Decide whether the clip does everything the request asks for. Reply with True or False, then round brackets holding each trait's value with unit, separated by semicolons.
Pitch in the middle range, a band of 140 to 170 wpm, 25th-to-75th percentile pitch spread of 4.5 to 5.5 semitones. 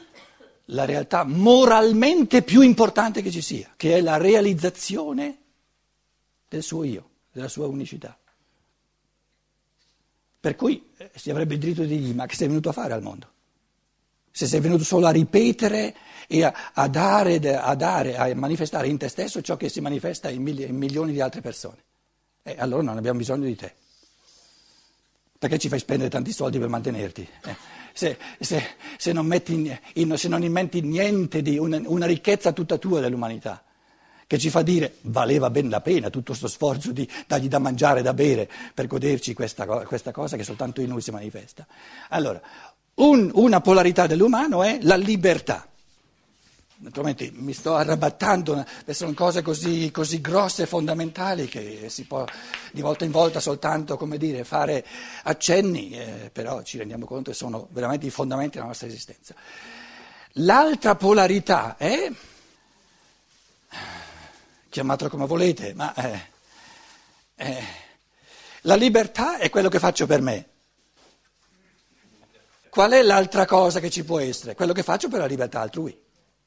True (160 Hz; 155 wpm; 5.2 semitones)